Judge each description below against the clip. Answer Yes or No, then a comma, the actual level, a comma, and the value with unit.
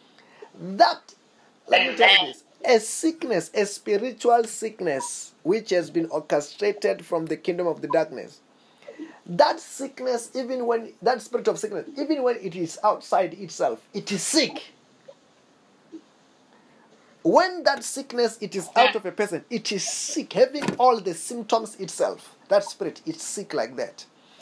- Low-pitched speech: No, high, 230 Hz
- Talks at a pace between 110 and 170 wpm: Yes, average, 150 wpm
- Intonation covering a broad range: Yes, wide, 6.5 semitones